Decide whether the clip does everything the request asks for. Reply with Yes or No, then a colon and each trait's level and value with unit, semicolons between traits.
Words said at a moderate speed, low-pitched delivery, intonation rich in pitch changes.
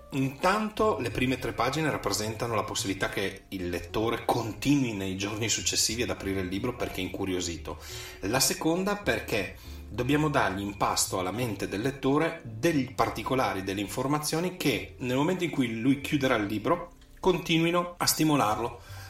Yes: average, 155 wpm; low, 120 Hz; wide, 7.0 semitones